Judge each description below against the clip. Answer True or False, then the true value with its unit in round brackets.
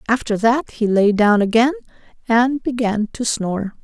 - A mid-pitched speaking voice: False (230 Hz)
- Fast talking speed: False (155 wpm)